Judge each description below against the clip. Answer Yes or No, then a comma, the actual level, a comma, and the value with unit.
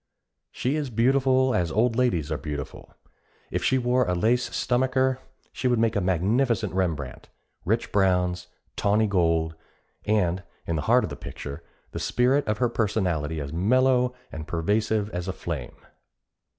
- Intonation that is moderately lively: No, wide, 6.4 semitones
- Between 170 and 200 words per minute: No, average, 155 wpm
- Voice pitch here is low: Yes, low, 105 Hz